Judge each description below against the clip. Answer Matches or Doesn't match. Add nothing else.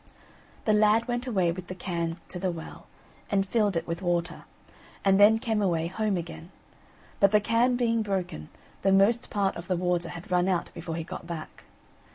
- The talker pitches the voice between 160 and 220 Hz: Matches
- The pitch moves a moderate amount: Matches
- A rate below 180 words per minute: Doesn't match